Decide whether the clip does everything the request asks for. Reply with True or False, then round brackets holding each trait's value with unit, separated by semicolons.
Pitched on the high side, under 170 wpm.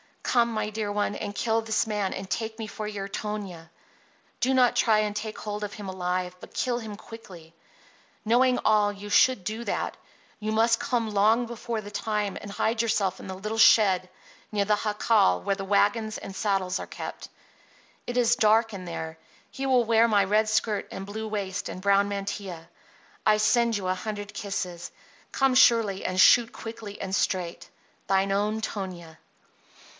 False (210 Hz; 180 wpm)